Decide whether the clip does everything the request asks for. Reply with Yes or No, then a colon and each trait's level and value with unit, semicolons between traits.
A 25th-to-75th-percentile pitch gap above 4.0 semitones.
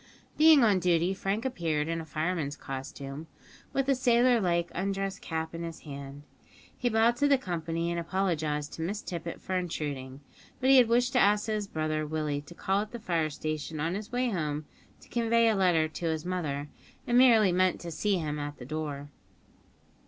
Yes: wide, 5.5 semitones